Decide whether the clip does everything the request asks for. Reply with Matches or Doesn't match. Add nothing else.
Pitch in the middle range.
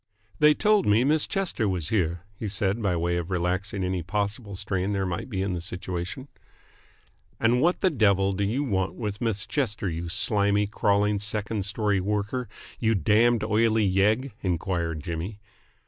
Doesn't match